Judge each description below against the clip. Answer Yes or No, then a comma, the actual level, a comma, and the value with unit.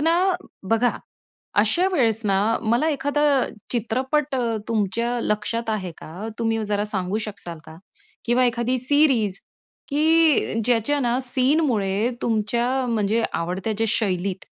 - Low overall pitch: No, high, 230 Hz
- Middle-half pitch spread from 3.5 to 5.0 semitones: Yes, average, 3.8 semitones